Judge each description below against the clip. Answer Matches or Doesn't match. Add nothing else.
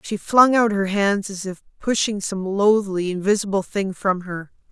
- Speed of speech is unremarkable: Matches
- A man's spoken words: Doesn't match